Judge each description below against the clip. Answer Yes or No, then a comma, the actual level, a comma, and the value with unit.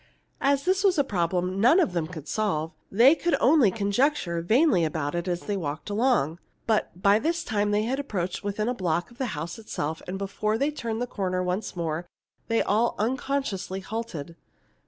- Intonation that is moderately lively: No, wide, 5.9 semitones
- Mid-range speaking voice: No, high, 205 Hz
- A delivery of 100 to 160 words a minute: No, average, 190 wpm